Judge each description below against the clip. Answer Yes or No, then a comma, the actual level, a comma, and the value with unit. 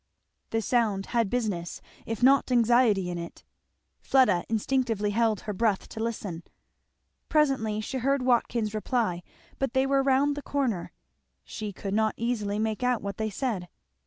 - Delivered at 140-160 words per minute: Yes, average, 155 wpm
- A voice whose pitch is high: Yes, high, 225 Hz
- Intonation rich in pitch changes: No, average, 3.6 semitones